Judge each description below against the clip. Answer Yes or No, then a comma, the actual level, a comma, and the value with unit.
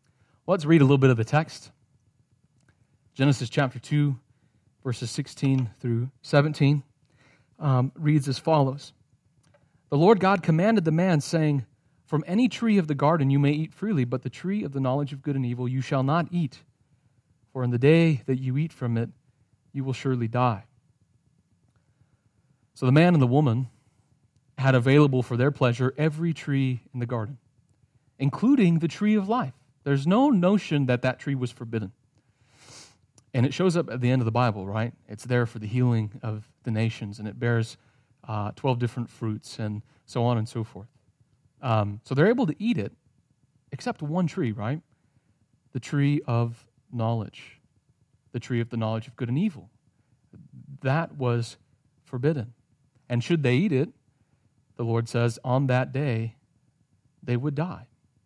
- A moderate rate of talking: Yes, average, 170 wpm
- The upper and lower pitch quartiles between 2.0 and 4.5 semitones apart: Yes, average, 3.2 semitones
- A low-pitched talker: Yes, low, 130 Hz